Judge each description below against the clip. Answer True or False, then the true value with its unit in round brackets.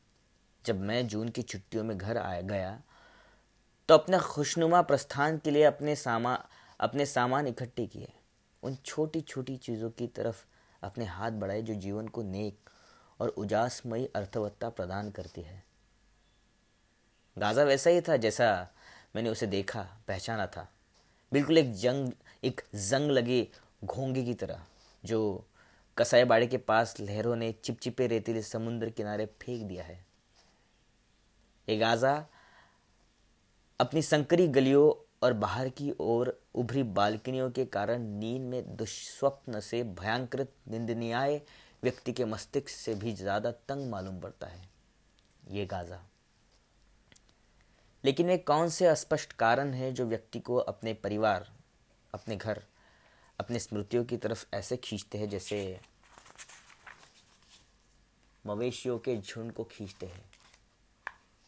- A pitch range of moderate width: True (3.6 semitones)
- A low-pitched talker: True (115 Hz)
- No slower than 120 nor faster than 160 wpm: True (130 wpm)